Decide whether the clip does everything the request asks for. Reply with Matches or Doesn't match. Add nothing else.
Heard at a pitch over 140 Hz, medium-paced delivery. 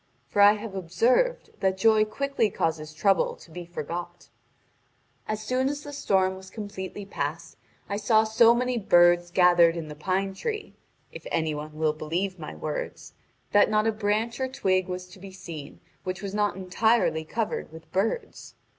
Matches